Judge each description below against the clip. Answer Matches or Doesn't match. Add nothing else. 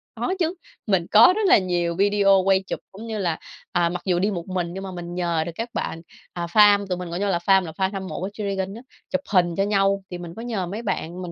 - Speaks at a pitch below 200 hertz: Matches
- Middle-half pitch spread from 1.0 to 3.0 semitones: Matches